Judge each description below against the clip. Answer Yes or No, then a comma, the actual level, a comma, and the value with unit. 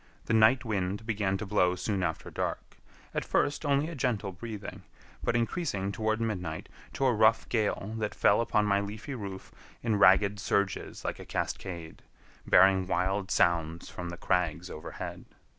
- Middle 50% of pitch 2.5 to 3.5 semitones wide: Yes, average, 3.0 semitones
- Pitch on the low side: Yes, low, 100 Hz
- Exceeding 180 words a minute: No, average, 160 wpm